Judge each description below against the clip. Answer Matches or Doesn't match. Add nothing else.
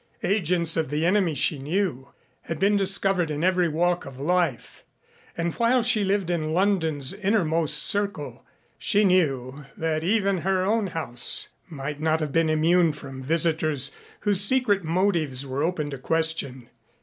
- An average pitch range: Matches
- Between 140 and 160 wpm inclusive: Matches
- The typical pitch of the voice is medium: Matches